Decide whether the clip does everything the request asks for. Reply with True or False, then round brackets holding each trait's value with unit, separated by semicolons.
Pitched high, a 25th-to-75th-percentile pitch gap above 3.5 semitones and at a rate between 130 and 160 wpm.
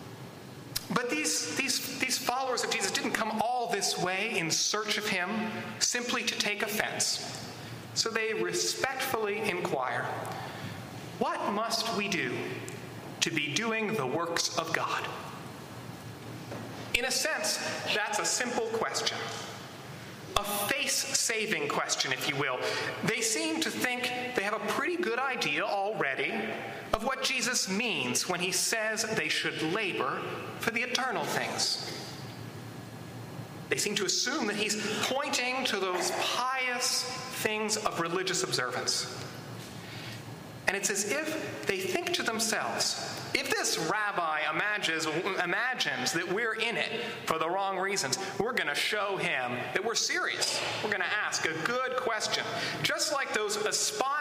True (220 Hz; 5.3 semitones; 140 wpm)